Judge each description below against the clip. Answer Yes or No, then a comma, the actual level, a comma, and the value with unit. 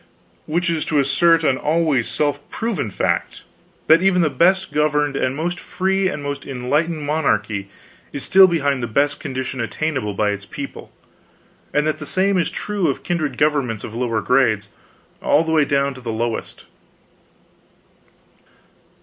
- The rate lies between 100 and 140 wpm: No, average, 160 wpm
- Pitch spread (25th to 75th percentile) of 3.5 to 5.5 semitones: Yes, average, 4.4 semitones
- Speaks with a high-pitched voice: No, medium, 145 Hz